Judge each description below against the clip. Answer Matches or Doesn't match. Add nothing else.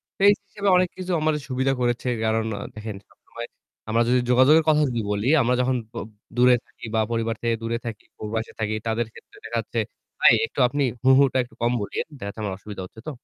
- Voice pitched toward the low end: Matches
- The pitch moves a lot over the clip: Doesn't match